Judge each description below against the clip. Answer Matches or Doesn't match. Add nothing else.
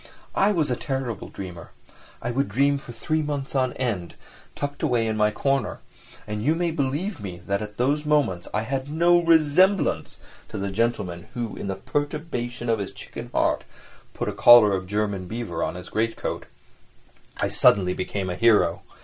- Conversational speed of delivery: Matches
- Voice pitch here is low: Matches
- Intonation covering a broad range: Matches